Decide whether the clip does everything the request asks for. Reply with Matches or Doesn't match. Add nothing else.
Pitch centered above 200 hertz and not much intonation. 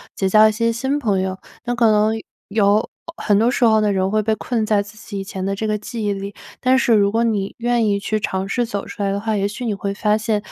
Matches